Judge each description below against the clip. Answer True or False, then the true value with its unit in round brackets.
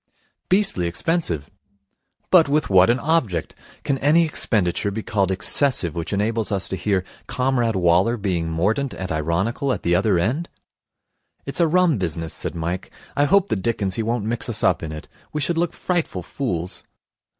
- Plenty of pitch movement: True (7.8 semitones)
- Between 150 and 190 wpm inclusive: True (170 wpm)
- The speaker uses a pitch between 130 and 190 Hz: False (105 Hz)